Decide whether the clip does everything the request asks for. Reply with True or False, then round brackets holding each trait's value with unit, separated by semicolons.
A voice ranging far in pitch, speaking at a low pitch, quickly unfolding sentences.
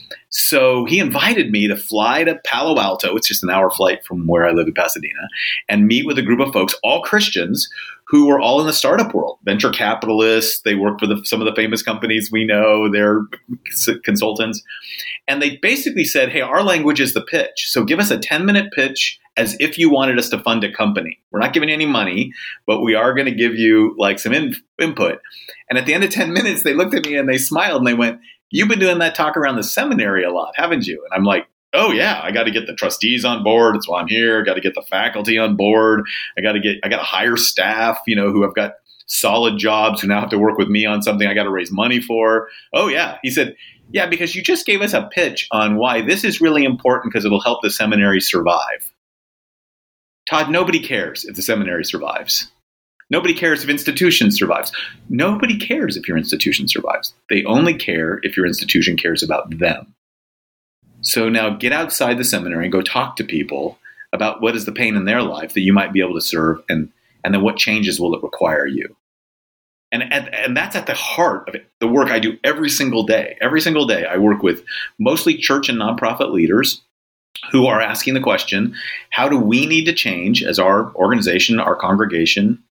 True (6.2 semitones; 115 Hz; 220 wpm)